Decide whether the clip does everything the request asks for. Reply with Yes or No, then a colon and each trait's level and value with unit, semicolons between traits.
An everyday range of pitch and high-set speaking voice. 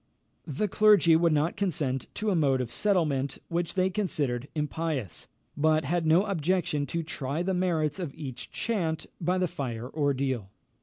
No: average, 4.5 semitones; medium, 160 Hz